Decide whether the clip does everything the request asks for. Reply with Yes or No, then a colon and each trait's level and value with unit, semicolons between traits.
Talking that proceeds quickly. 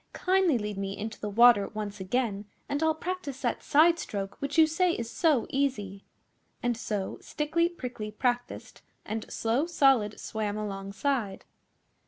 No: average, 150 wpm